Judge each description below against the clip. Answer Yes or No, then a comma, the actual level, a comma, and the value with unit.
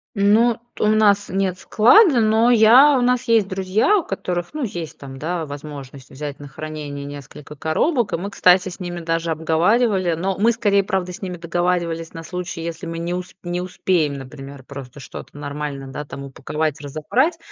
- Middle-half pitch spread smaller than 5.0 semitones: No, average, 5.3 semitones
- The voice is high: No, medium, 175 Hz